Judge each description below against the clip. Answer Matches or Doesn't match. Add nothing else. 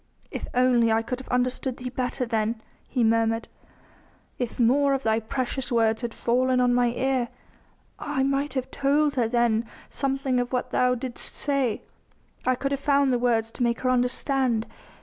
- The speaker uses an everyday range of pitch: Doesn't match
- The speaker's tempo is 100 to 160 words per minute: Doesn't match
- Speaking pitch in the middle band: Doesn't match